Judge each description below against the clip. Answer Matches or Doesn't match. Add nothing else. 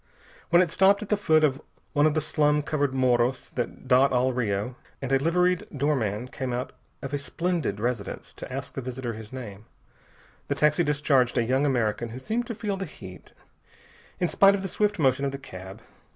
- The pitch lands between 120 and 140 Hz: Matches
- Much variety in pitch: Doesn't match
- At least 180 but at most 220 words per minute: Matches